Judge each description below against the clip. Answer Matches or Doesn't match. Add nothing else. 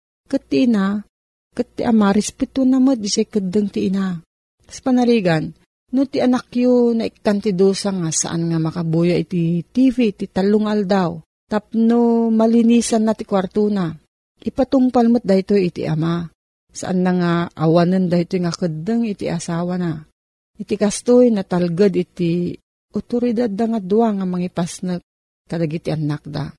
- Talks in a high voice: Matches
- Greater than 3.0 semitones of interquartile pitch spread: Matches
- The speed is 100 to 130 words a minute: Doesn't match